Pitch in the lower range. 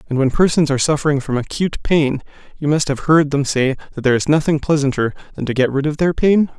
No: medium, 145 Hz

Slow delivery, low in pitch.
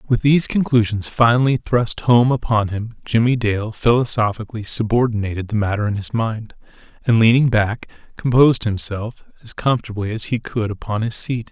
No: average, 155 wpm; low, 110 Hz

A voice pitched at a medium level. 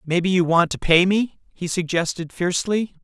Yes: medium, 180 Hz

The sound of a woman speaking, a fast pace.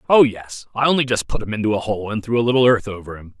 No: male; fast, 300 wpm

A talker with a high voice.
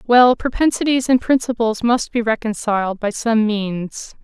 Yes: high, 230 Hz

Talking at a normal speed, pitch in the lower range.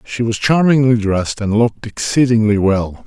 Yes: average, 155 wpm; low, 115 Hz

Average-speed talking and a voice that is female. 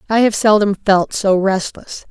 Yes: average, 170 wpm; female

